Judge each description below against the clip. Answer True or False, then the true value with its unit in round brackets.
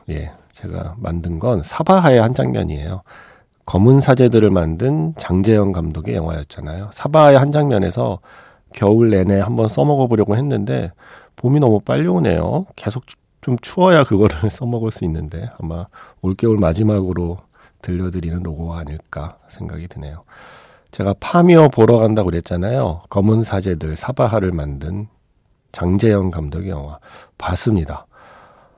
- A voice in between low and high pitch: False (100 Hz)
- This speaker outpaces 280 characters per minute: True (315 characters per minute)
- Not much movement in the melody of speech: False (5.5 semitones)